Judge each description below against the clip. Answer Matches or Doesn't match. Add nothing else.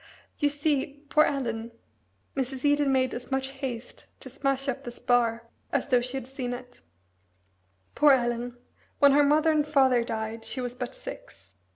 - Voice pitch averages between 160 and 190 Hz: Doesn't match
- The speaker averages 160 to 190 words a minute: Matches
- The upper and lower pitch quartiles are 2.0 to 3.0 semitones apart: Matches